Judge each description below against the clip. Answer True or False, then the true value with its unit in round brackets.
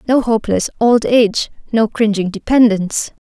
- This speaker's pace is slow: True (130 wpm)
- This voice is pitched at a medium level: False (220 Hz)